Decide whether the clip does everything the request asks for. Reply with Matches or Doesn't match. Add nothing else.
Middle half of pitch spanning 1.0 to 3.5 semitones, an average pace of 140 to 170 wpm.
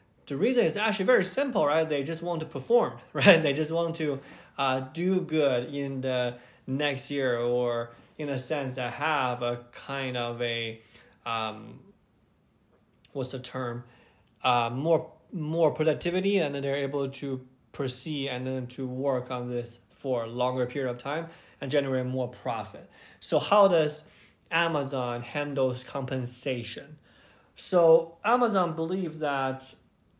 Doesn't match